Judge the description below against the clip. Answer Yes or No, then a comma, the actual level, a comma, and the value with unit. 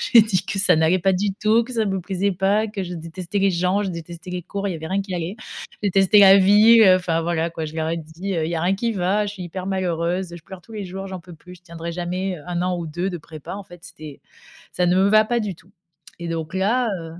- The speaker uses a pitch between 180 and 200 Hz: Yes, medium, 185 Hz